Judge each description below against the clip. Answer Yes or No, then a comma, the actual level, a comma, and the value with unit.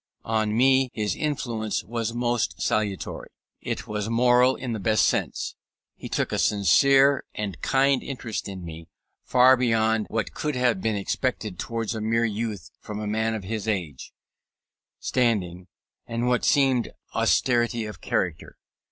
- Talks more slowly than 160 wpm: Yes, average, 150 wpm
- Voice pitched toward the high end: No, low, 115 Hz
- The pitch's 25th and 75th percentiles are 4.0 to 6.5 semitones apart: No, average, 2.8 semitones